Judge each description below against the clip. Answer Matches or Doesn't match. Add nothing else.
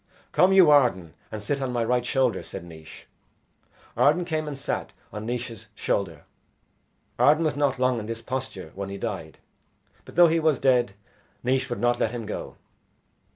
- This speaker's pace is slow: Doesn't match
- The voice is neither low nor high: Doesn't match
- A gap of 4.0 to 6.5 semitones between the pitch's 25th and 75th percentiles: Matches